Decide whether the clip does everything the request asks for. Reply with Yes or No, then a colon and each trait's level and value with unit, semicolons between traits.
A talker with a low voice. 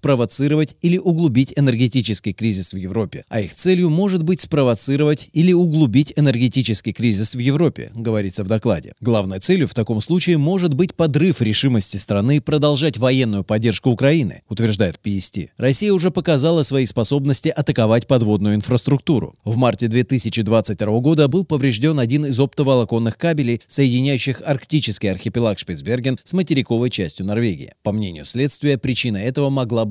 Yes: low, 130 Hz